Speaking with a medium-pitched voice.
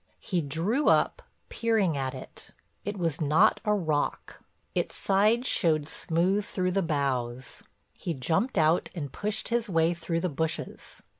Yes: medium, 170 Hz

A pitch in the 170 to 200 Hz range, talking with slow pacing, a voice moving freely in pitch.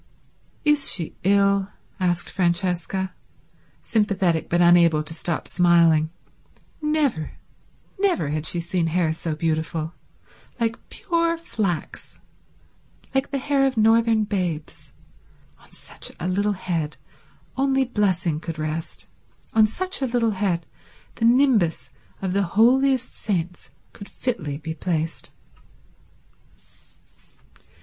Yes: medium, 185 Hz; slow, 110 wpm; wide, 5.8 semitones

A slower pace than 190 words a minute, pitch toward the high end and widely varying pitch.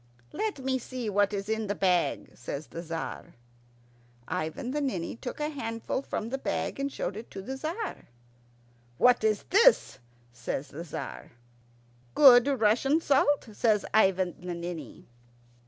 Yes: average, 150 wpm; high, 220 Hz; wide, 6.9 semitones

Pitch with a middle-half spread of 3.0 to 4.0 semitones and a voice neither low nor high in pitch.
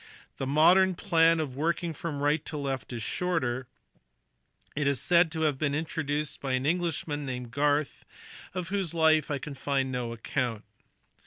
Yes: average, 3.5 semitones; medium, 145 Hz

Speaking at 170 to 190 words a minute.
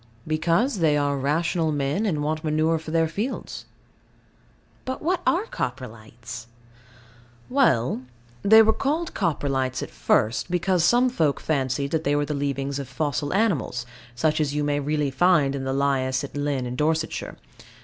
No: average, 155 wpm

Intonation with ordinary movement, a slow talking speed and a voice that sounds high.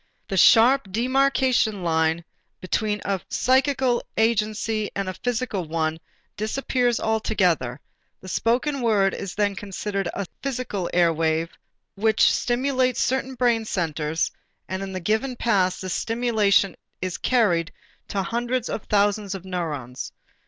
Yes: average, 4.7 semitones; slow, 125 wpm; high, 210 Hz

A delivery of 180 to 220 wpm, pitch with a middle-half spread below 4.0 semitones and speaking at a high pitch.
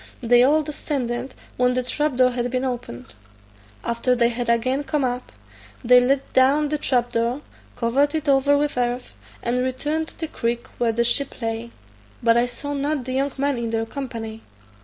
Yes: average, 185 wpm; average, 2.9 semitones; very high, 250 Hz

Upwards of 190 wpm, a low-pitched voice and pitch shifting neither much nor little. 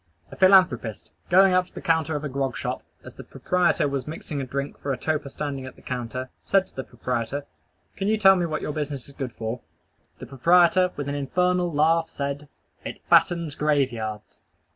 No: average, 200 wpm; medium, 145 Hz; average, 4.6 semitones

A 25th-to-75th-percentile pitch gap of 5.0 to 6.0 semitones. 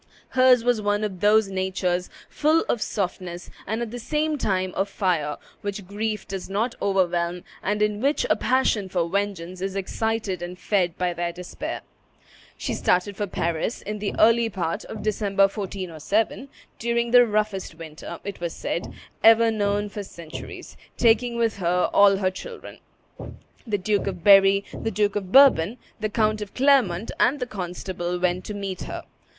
No: average, 3.4 semitones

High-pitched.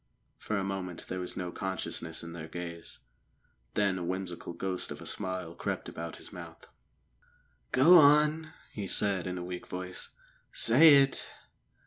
No: very low, 95 Hz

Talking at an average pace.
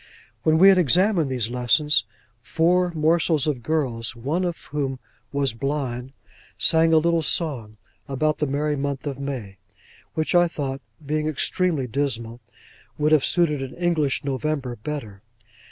Yes: average, 145 wpm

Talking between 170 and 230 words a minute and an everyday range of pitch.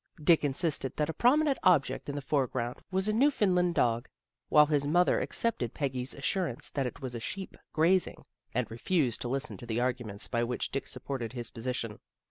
No: average, 190 wpm; wide, 6.4 semitones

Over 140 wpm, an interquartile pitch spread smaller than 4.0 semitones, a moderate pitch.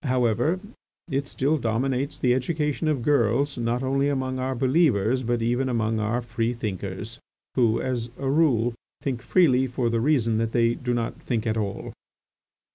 No: average, 165 wpm; average, 2.8 semitones; low, 125 Hz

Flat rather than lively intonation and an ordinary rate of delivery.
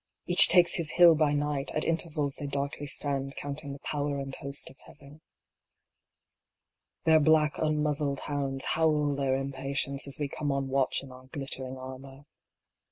Yes: narrow, 1.8 semitones; average, 160 wpm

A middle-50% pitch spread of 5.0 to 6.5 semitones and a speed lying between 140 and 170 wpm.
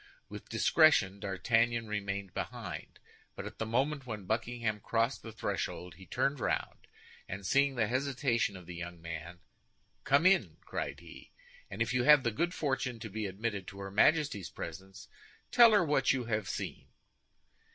Yes: wide, 5.4 semitones; average, 165 wpm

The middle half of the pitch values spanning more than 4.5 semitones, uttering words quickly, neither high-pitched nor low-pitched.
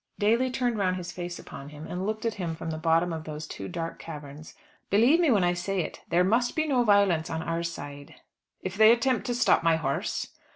Yes: average, 5.2 semitones; fast, 225 wpm; medium, 180 Hz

